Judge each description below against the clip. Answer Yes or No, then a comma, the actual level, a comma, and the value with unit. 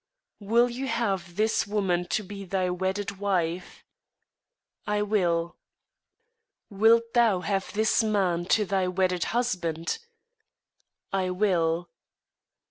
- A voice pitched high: Yes, high, 195 Hz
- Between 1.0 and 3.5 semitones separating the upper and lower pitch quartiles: Yes, average, 2.9 semitones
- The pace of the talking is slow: Yes, slow, 105 wpm